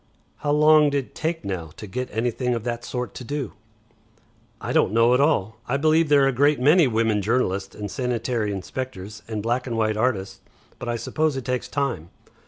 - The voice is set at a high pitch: No, low, 125 Hz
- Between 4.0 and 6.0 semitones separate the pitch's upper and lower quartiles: Yes, average, 4.4 semitones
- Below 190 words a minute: No, average, 195 wpm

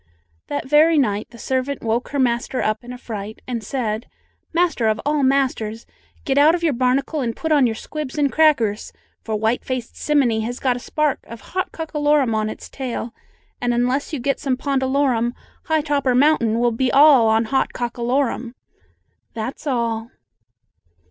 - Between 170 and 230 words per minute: Yes, average, 175 wpm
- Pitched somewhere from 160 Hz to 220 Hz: No, very high, 255 Hz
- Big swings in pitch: No, average, 3.7 semitones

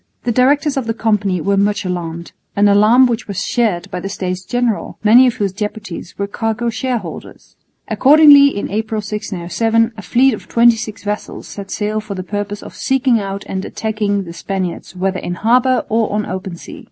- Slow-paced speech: No, average, 190 wpm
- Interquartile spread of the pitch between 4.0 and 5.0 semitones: No, average, 3.1 semitones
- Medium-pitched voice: No, high, 210 Hz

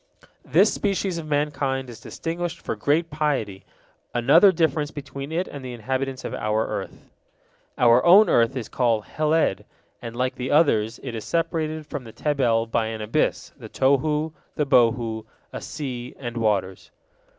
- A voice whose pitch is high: No, low, 135 Hz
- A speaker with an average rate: Yes, average, 160 wpm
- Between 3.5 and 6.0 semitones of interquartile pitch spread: Yes, average, 4.8 semitones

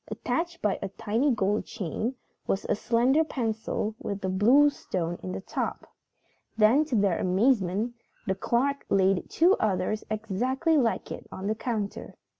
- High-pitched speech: Yes, high, 220 Hz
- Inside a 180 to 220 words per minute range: No, average, 155 wpm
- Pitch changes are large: No, average, 5.0 semitones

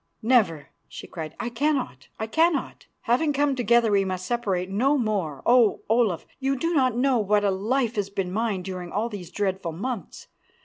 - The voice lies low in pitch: No, high, 220 Hz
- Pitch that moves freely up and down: No, average, 5.0 semitones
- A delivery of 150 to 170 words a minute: No, average, 180 wpm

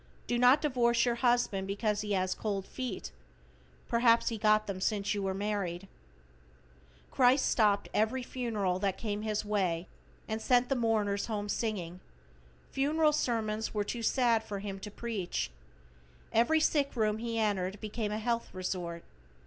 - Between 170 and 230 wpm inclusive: No, average, 155 wpm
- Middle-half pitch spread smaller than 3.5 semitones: Yes, average, 3.0 semitones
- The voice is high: Yes, high, 215 Hz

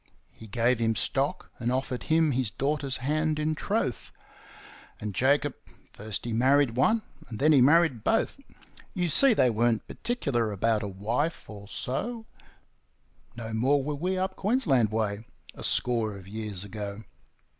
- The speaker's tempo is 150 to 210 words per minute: Yes, average, 155 wpm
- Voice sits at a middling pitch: No, low, 125 Hz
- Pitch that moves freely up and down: Yes, wide, 5.7 semitones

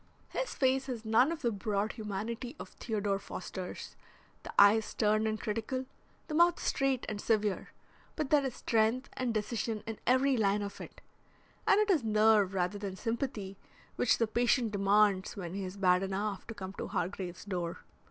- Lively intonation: No, average, 3.6 semitones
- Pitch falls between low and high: No, high, 215 Hz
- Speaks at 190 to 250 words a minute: No, average, 180 wpm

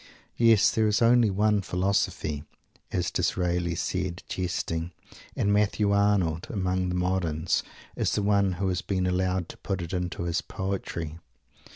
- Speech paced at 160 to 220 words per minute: No, average, 150 wpm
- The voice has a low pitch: Yes, very low, 95 Hz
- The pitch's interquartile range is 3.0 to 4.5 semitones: No, narrow, 2.4 semitones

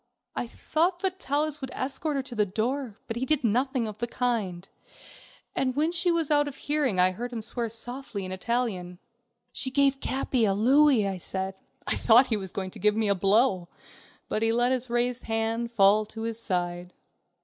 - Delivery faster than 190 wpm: Yes, average, 200 wpm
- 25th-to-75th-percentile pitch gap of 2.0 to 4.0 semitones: No, average, 4.6 semitones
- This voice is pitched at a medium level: No, high, 235 Hz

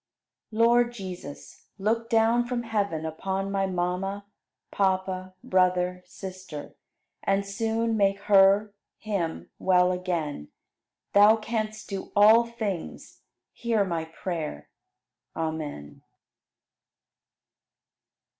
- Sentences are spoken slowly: Yes, slow, 95 wpm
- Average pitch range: Yes, average, 3.2 semitones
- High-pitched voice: Yes, high, 195 Hz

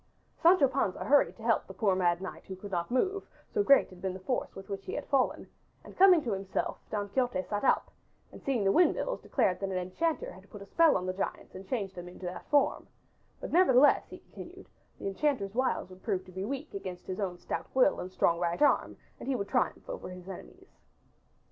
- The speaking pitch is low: No, high, 200 Hz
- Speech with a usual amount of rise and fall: No, wide, 6.6 semitones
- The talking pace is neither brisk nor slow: No, fast, 225 wpm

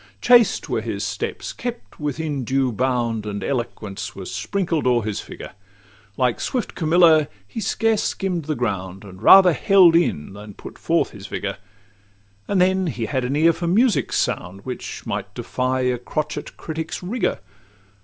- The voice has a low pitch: No, medium, 145 Hz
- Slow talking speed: No, average, 165 wpm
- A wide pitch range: Yes, wide, 7.3 semitones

